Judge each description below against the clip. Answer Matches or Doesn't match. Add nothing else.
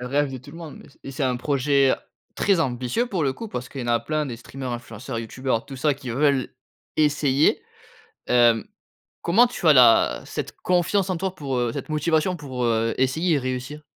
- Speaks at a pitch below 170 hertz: Matches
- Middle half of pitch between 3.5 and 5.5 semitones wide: Matches